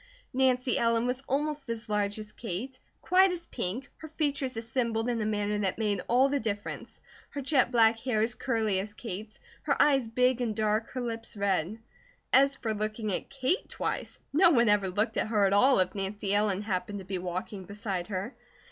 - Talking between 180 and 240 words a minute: Yes, average, 195 wpm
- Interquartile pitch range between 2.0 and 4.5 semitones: Yes, average, 3.8 semitones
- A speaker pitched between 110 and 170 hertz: No, high, 225 Hz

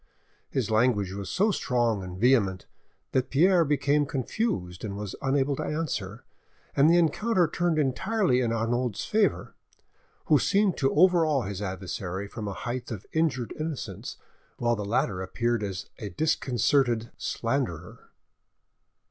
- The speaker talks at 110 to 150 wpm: Yes, average, 140 wpm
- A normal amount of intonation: No, wide, 6.9 semitones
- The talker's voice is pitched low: Yes, low, 125 Hz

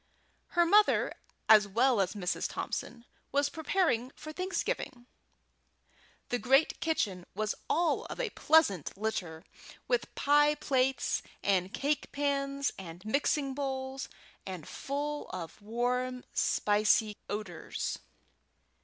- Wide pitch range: Yes, wide, 5.9 semitones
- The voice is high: Yes, very high, 255 Hz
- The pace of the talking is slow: Yes, slow, 110 wpm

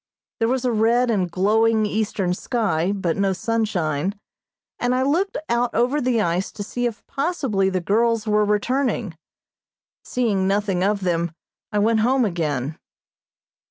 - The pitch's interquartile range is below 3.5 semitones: No, average, 4.0 semitones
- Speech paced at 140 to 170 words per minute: Yes, average, 150 wpm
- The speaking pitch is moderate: No, high, 210 Hz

